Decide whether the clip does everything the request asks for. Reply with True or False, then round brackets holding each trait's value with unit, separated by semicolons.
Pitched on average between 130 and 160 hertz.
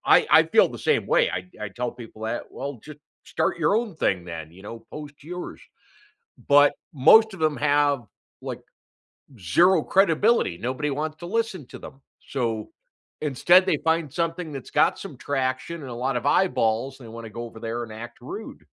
True (140 Hz)